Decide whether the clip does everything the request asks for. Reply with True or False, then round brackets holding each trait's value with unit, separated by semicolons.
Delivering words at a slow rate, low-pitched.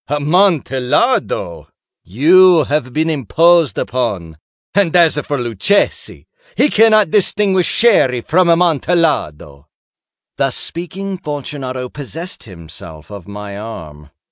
False (100 wpm; 145 Hz)